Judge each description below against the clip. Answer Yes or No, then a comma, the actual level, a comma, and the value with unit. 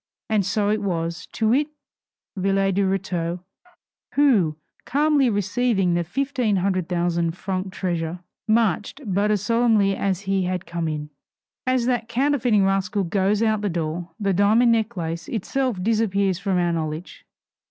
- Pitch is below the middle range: No, high, 195 Hz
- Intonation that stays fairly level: No, average, 4.0 semitones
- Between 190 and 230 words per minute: No, average, 150 wpm